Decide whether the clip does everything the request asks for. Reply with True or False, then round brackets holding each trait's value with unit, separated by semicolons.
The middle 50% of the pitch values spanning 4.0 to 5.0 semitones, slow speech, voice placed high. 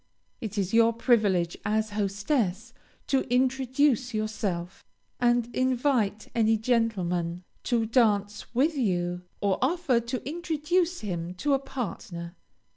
True (4.6 semitones; 120 wpm; 225 Hz)